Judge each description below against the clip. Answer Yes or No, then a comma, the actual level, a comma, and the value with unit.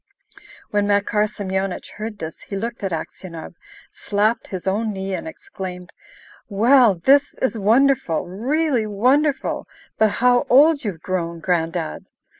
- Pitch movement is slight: No, average, 4.9 semitones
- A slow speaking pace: Yes, slow, 130 wpm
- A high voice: Yes, high, 205 Hz